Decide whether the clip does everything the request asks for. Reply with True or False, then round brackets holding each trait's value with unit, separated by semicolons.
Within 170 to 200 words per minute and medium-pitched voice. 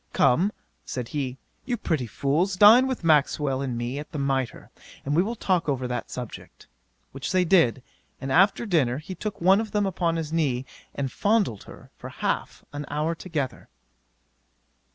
True (175 wpm; 155 Hz)